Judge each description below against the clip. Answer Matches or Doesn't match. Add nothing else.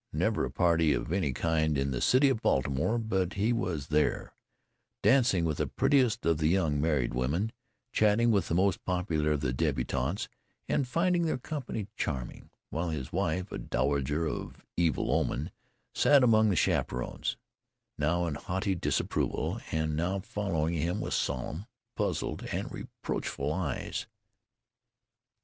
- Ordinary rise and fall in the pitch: Doesn't match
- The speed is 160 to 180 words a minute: Doesn't match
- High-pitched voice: Doesn't match